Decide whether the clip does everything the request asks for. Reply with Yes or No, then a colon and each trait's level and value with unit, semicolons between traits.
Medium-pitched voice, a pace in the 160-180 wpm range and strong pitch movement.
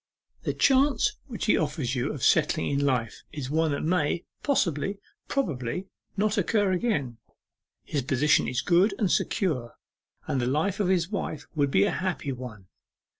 Yes: medium, 155 Hz; average, 165 wpm; wide, 6.6 semitones